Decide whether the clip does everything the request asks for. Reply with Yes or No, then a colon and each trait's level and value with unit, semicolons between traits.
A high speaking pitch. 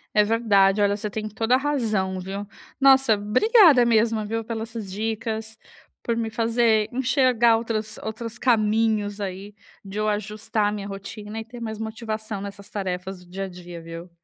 Yes: high, 215 Hz